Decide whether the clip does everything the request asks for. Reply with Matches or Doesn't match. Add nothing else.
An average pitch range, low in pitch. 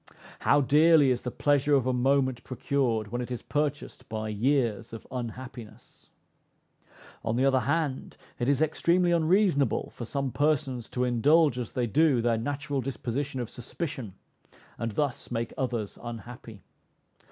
Matches